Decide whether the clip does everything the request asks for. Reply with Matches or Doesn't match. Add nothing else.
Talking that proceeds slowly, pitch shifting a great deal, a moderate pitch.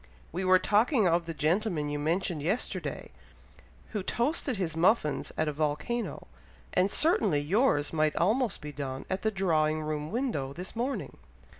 Doesn't match